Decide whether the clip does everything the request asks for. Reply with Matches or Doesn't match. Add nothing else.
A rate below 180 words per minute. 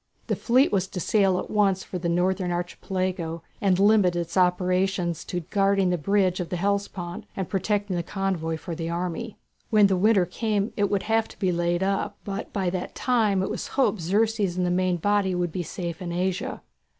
Doesn't match